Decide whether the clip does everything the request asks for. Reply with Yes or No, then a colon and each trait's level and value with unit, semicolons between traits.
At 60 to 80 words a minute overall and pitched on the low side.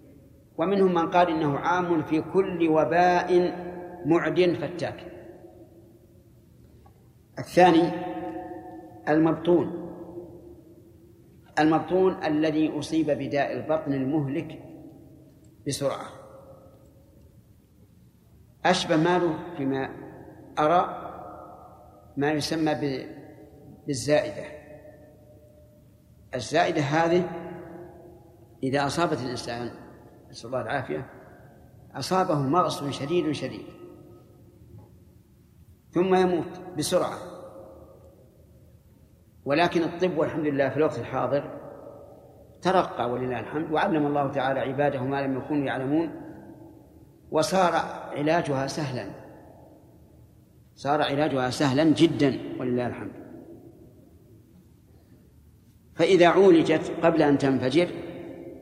No: average, 75 wpm; medium, 150 Hz